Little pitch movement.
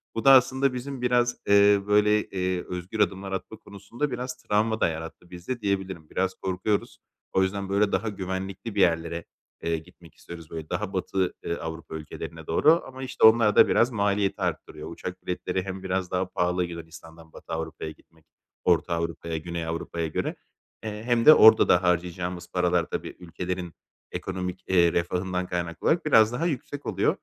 No: average, 3.7 semitones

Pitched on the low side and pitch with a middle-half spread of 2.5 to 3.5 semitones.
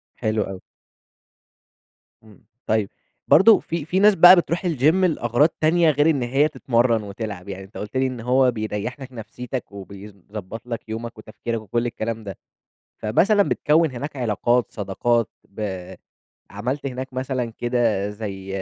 No: low, 120 Hz; average, 4.4 semitones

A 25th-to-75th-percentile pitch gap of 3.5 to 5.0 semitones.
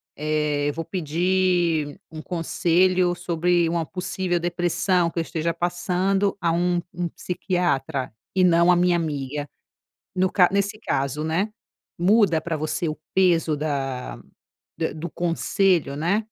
No: narrow, 2.5 semitones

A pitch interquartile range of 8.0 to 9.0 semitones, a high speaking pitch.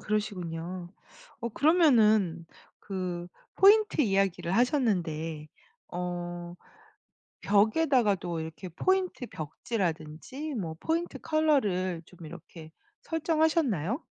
Yes: wide, 8.4 semitones; high, 195 Hz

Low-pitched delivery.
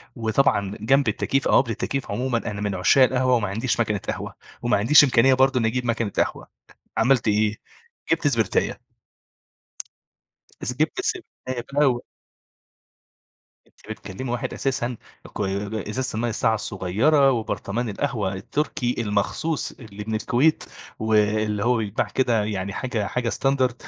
Yes: low, 115 Hz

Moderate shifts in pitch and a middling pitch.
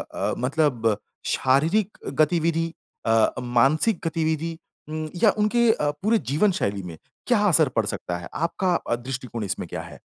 No: wide, 5.7 semitones; medium, 155 Hz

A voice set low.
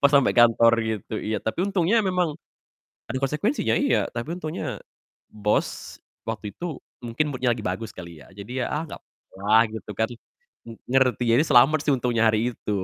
Yes: low, 125 Hz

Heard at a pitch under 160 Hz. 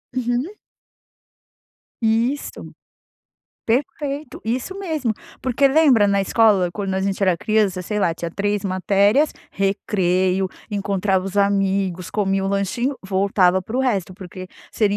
No: high, 200 Hz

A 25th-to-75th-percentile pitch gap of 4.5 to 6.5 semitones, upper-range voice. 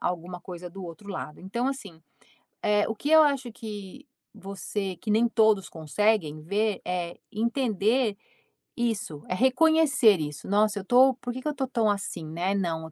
Yes: average, 4.8 semitones; high, 205 Hz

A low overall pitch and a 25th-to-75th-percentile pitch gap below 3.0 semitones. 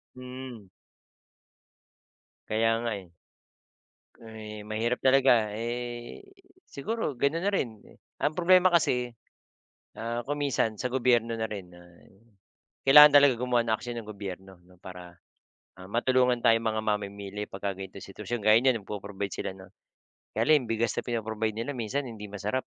No: low, 115 Hz; average, 3.5 semitones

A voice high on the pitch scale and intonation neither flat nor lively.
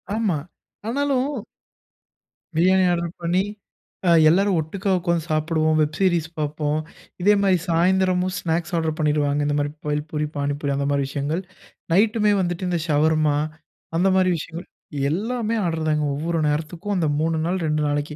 No: medium, 165 Hz; average, 3.5 semitones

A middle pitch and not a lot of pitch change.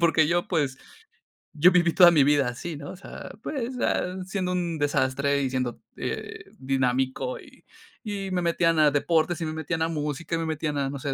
No: medium, 160 Hz; average, 3.7 semitones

